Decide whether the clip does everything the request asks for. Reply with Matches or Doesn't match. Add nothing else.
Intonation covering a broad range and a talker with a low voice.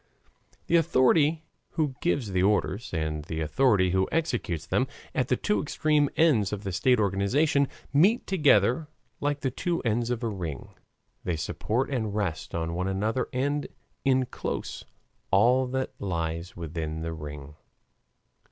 Matches